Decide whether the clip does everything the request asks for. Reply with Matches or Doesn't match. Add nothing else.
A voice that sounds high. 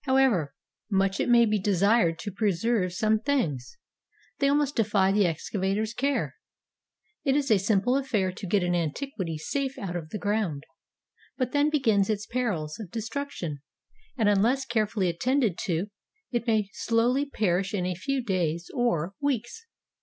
Matches